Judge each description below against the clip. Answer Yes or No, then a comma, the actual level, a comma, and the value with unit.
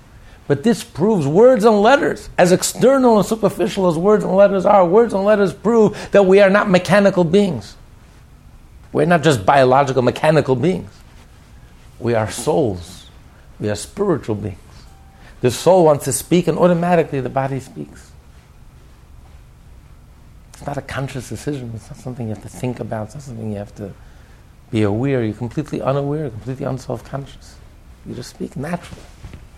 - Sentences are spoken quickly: No, average, 160 wpm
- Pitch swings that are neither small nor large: No, wide, 8.6 semitones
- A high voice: No, low, 135 Hz